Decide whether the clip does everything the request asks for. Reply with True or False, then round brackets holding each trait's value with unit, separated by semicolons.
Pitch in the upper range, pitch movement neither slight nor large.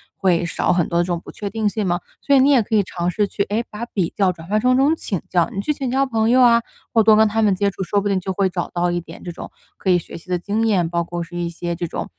True (195 Hz; 4.1 semitones)